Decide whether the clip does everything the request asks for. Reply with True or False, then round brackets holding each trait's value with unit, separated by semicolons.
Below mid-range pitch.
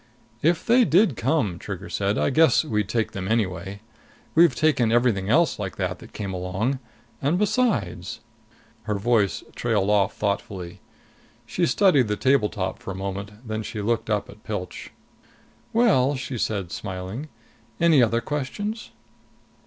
True (110 Hz)